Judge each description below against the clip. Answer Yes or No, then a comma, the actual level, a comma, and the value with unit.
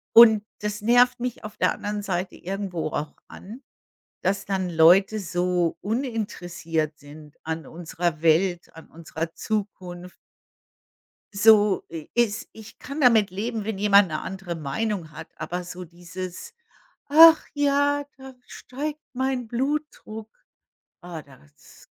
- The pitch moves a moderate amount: Yes, average, 4.9 semitones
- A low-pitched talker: No, high, 195 Hz